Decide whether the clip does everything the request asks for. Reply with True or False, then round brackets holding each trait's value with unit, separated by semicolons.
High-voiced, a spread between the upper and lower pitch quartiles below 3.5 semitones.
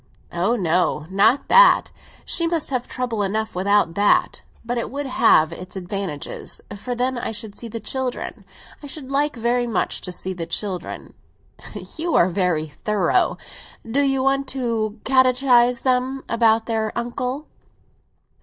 False (235 Hz; 4.6 semitones)